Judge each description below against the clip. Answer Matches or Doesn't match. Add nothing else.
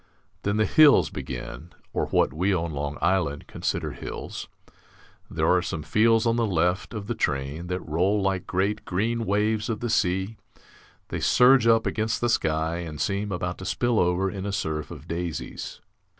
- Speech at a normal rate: Matches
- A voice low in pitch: Matches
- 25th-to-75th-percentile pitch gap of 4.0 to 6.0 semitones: Matches